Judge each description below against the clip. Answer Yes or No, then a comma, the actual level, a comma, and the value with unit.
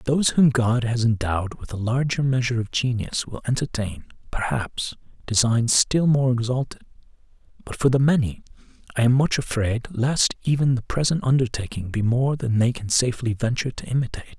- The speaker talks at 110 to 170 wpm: Yes, average, 165 wpm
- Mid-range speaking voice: No, low, 120 Hz